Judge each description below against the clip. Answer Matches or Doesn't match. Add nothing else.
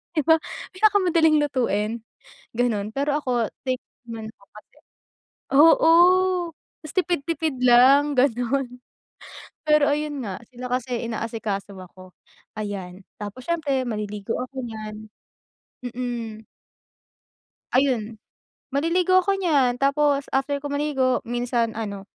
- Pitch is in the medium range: Doesn't match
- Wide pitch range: Doesn't match